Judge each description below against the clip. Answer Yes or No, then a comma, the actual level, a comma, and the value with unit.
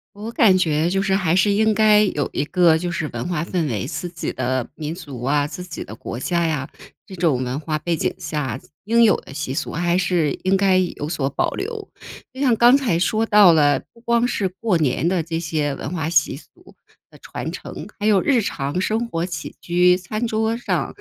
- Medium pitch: Yes, medium, 175 Hz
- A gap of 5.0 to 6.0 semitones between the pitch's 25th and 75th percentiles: Yes, wide, 5.4 semitones